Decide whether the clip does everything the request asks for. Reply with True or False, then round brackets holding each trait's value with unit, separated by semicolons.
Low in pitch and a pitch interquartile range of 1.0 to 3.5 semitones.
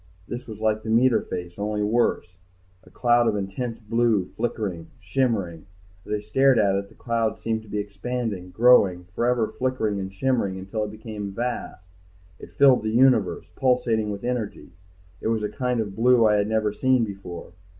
True (110 Hz; 3.1 semitones)